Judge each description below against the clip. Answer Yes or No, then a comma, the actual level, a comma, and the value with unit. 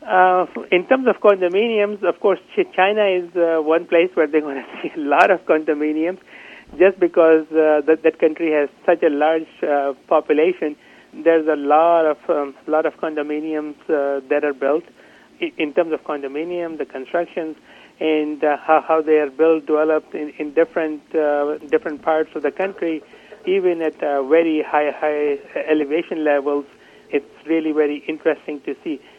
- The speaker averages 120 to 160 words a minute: No, average, 170 wpm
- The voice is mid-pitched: Yes, medium, 155 Hz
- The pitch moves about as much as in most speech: No, narrow, 2.3 semitones